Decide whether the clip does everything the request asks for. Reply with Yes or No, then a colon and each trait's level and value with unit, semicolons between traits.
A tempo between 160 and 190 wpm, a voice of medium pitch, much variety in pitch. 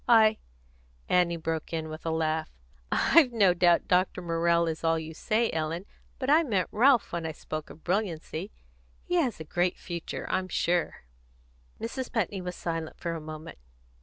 No: average, 175 wpm; medium, 170 Hz; average, 4.4 semitones